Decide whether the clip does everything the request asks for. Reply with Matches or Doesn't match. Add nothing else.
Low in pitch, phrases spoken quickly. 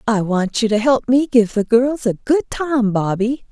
Doesn't match